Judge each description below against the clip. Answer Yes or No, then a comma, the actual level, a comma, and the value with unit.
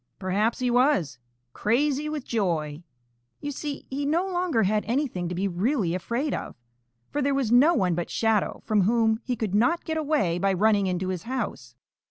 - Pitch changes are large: Yes, wide, 7.1 semitones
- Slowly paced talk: No, average, 185 wpm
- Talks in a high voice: Yes, high, 225 Hz